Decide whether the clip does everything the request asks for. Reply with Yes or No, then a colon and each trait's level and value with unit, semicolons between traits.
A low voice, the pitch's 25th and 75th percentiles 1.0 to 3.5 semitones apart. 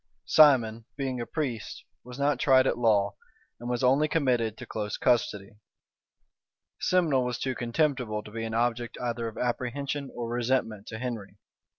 Yes: low, 120 Hz; average, 2.8 semitones